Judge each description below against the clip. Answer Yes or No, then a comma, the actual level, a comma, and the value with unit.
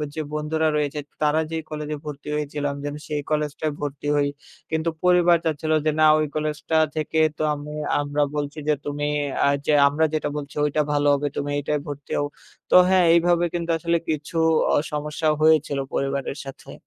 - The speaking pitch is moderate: Yes, medium, 150 Hz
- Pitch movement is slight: Yes, narrow, 1.5 semitones